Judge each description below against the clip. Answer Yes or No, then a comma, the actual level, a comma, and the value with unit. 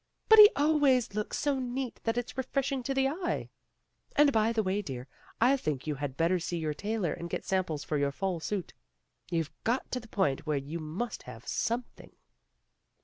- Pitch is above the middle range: Yes, high, 210 Hz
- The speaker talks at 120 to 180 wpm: No, average, 195 wpm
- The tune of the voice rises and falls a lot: Yes, wide, 8.3 semitones